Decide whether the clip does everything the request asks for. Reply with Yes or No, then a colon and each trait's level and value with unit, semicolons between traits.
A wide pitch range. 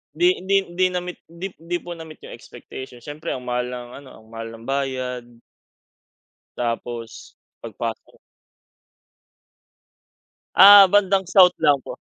Yes: wide, 6.6 semitones